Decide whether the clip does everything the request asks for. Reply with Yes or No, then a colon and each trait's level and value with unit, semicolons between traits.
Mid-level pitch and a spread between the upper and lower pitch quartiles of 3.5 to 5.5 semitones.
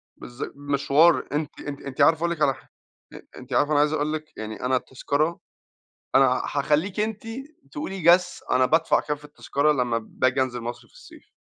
Yes: medium, 145 Hz; average, 3.8 semitones